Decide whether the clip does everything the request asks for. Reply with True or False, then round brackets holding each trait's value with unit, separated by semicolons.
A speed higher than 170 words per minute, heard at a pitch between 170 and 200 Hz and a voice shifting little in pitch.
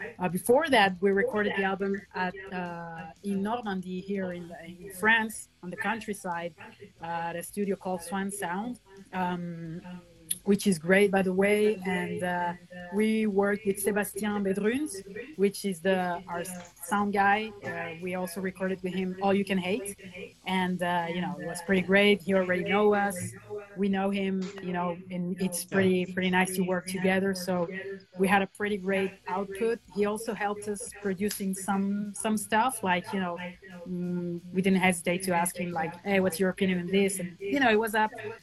True (185 wpm; 190 Hz; 2.1 semitones)